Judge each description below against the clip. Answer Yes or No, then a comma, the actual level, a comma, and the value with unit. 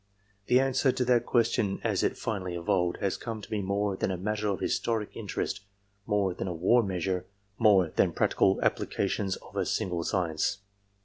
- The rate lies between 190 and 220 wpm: No, average, 180 wpm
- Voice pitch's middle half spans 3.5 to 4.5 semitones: No, average, 3.1 semitones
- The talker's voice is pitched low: Yes, low, 100 Hz